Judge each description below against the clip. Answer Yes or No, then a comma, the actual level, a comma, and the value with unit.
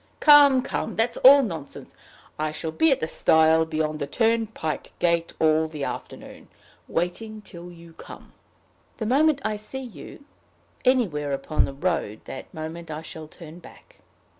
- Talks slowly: No, average, 155 wpm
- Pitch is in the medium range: Yes, medium, 170 Hz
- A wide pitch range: Yes, wide, 6.4 semitones